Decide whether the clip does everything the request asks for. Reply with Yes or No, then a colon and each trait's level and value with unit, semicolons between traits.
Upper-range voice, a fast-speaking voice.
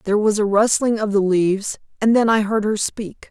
Yes: high, 210 Hz; fast, 220 wpm